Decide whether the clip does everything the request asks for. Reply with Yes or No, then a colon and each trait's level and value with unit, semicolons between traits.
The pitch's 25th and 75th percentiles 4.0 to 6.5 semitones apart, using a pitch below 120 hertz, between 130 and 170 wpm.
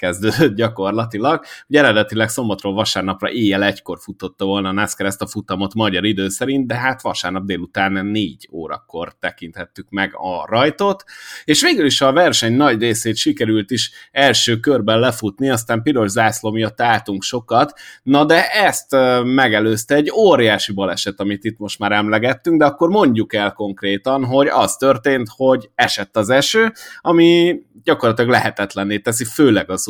Yes: average, 4.7 semitones; low, 110 Hz; fast, 155 wpm